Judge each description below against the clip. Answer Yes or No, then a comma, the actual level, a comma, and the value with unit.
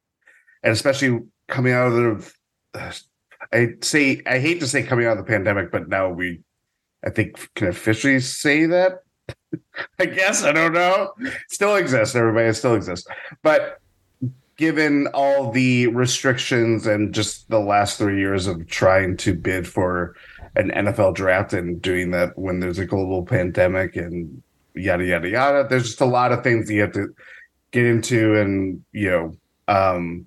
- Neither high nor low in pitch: No, low, 110 Hz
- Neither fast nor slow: Yes, average, 165 wpm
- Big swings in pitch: Yes, wide, 5.7 semitones